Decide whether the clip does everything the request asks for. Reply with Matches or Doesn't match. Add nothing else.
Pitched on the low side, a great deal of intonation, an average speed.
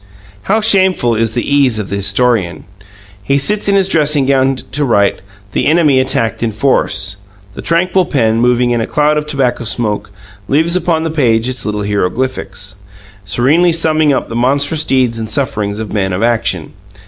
Matches